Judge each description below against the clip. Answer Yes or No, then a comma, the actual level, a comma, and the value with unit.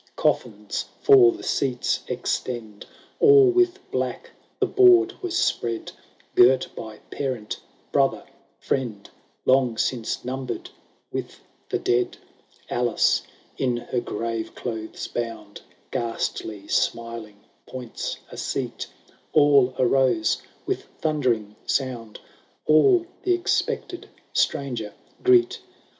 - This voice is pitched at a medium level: No, low, 125 Hz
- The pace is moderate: No, slow, 100 wpm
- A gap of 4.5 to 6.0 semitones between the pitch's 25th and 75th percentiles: Yes, average, 5.3 semitones